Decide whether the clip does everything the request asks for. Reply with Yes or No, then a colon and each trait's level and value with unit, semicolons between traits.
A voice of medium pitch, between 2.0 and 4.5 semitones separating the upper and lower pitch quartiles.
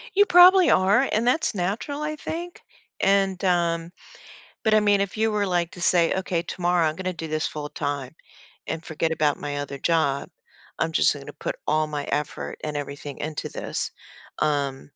No: medium, 170 Hz; average, 5.1 semitones